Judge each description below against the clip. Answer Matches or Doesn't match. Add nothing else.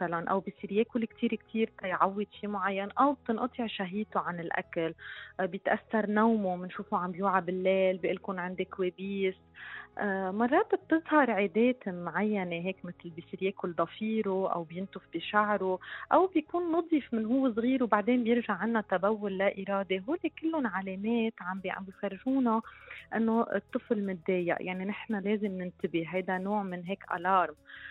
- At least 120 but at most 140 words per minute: Matches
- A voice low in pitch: Doesn't match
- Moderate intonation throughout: Matches